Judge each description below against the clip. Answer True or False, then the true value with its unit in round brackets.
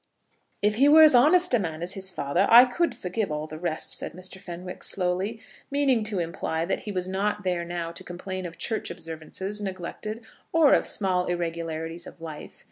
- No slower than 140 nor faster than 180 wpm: False (195 wpm)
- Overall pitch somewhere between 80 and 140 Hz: False (185 Hz)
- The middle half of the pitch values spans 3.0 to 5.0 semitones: True (4.2 semitones)